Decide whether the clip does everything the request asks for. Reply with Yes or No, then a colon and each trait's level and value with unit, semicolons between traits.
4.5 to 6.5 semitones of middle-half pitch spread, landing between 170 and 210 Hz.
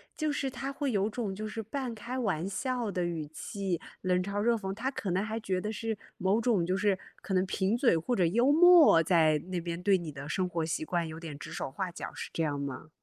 Yes: average, 5.2 semitones; high, 195 Hz